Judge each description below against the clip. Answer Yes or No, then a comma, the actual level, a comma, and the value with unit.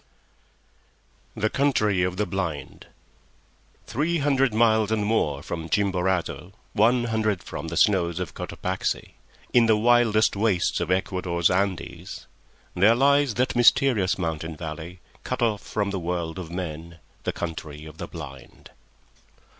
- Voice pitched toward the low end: Yes, very low, 95 Hz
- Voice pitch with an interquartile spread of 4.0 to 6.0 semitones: Yes, average, 4.7 semitones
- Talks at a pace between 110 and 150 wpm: Yes, average, 140 wpm